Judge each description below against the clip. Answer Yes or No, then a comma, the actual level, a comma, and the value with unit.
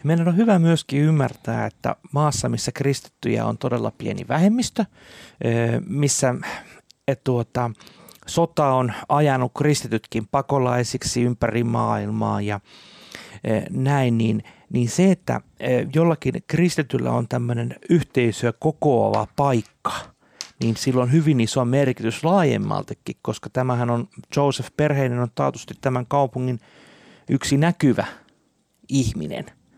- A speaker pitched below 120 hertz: No, low, 130 Hz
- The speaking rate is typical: Yes, average, 110 wpm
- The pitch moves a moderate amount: Yes, average, 3.7 semitones